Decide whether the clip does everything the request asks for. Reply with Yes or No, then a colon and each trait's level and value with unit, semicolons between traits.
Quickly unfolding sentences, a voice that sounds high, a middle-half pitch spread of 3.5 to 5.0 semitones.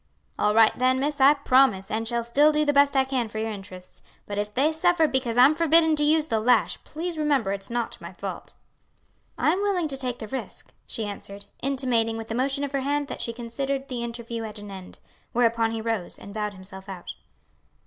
Yes: fast, 220 wpm; high, 245 Hz; average, 4.5 semitones